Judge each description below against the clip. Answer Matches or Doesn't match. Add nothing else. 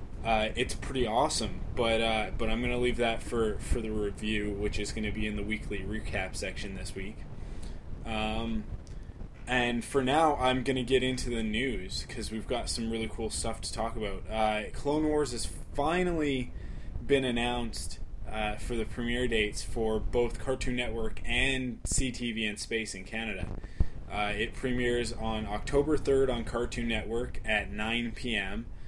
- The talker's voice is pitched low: Matches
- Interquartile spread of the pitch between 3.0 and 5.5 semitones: Doesn't match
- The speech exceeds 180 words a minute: Doesn't match